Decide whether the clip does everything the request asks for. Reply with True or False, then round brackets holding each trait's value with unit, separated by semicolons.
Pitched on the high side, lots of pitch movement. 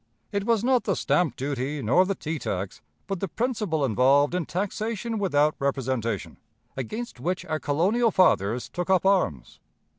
False (170 Hz; 6.8 semitones)